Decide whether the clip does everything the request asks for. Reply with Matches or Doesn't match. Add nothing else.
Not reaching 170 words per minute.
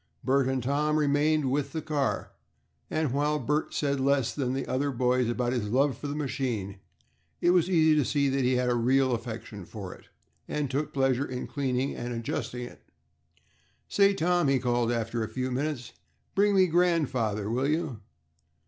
Doesn't match